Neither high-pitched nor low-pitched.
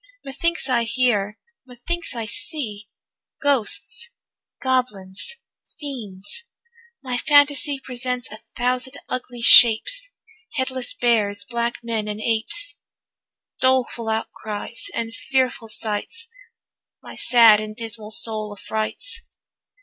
No: high, 240 Hz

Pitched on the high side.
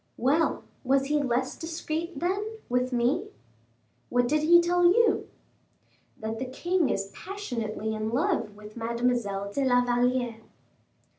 Yes: very high, 255 Hz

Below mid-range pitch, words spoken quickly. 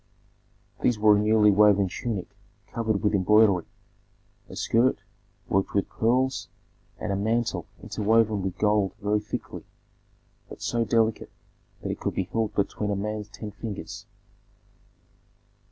No: low, 105 Hz; slow, 135 wpm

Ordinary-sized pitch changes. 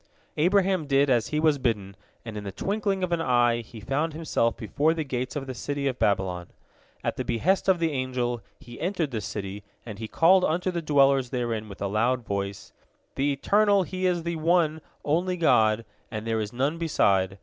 No: wide, 6.8 semitones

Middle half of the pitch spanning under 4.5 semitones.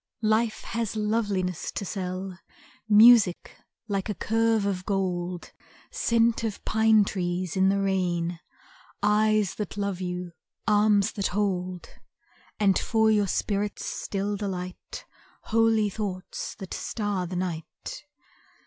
Yes: average, 2.8 semitones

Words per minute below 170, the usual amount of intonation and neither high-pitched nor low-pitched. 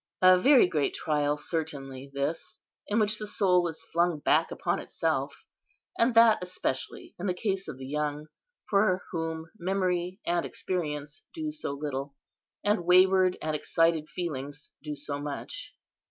Yes: average, 150 wpm; average, 4.1 semitones; medium, 170 Hz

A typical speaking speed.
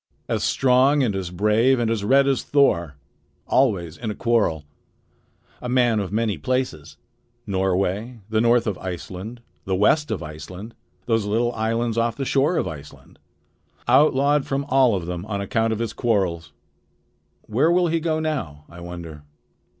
Yes: average, 160 wpm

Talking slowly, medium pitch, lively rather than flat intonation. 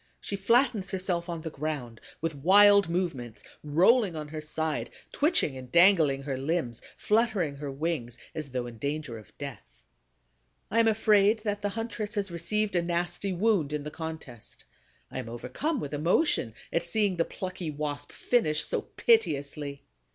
No: average, 160 wpm; medium, 165 Hz; wide, 6.0 semitones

